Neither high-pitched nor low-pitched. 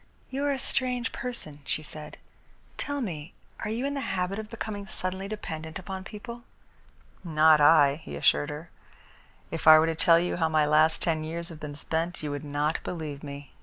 Yes: medium, 165 Hz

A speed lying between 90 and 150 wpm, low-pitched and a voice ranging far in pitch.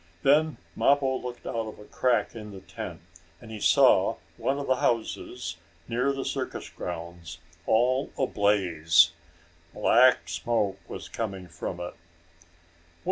Yes: slow, 135 wpm; low, 110 Hz; wide, 6.4 semitones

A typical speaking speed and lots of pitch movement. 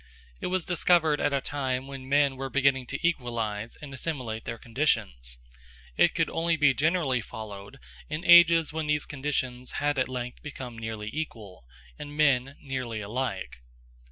No: average, 155 wpm; average, 4.1 semitones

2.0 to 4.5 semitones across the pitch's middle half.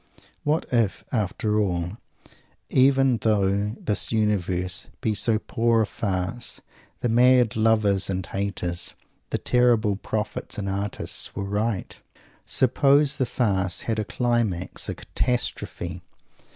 Yes: average, 3.4 semitones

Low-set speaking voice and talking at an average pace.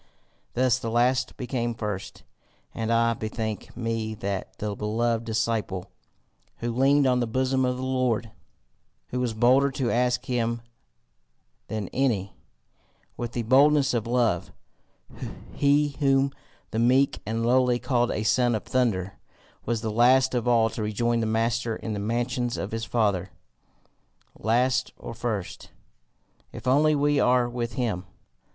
Yes: low, 120 Hz; average, 145 wpm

